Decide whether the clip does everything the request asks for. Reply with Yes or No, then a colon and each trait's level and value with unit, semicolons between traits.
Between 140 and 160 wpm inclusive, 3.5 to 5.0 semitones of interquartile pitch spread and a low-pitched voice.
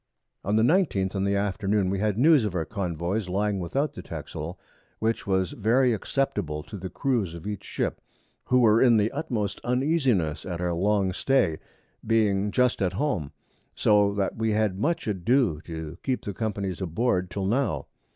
No: average, 175 wpm; average, 4.1 semitones; low, 105 Hz